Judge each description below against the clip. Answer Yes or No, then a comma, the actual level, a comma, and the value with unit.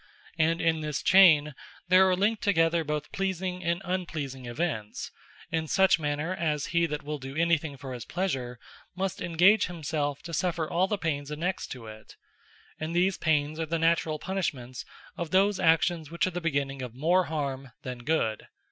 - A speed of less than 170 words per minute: No, average, 180 wpm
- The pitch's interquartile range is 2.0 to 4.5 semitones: Yes, average, 3.6 semitones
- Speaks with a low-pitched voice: No, medium, 160 Hz